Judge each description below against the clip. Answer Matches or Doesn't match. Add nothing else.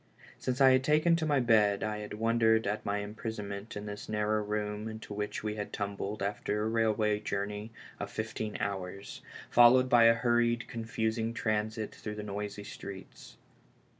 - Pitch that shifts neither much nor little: Doesn't match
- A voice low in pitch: Matches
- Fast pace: Doesn't match